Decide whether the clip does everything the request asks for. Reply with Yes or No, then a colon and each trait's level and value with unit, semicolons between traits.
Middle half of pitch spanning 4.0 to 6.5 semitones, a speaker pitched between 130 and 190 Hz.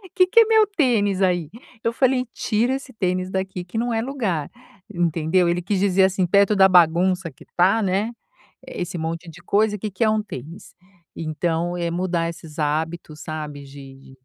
Yes: average, 4.3 semitones; medium, 185 Hz